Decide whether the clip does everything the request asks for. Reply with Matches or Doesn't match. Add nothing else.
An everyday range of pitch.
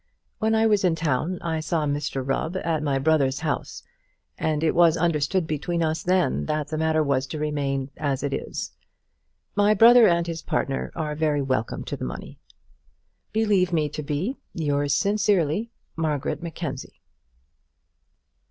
Matches